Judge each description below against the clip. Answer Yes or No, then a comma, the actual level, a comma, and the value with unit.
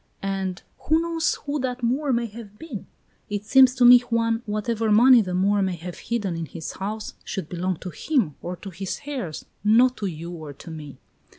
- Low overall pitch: No, high, 210 Hz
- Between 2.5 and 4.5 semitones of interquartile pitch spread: No, average, 5.2 semitones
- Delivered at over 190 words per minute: Yes, average, 200 wpm